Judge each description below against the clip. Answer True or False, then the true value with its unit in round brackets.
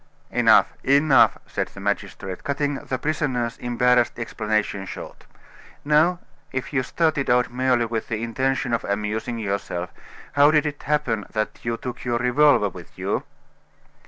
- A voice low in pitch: True (125 Hz)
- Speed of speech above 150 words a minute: False (145 wpm)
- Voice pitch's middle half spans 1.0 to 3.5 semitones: False (4.3 semitones)